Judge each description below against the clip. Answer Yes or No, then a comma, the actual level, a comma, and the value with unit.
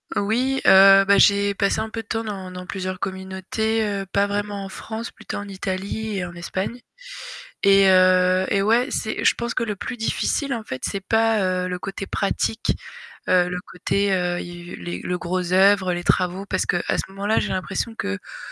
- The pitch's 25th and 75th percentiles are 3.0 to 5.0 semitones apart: No, narrow, 2.5 semitones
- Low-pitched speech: No, high, 195 Hz